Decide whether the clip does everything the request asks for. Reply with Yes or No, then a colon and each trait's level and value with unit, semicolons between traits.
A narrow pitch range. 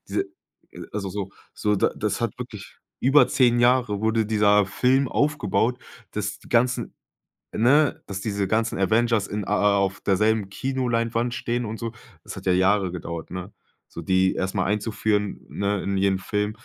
No: average, 3.2 semitones